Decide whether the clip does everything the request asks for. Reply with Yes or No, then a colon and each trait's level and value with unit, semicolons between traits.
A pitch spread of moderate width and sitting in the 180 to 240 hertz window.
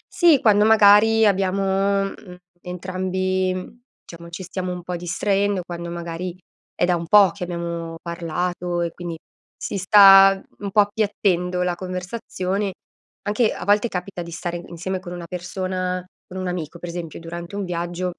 No: narrow, 2.2 semitones; medium, 185 Hz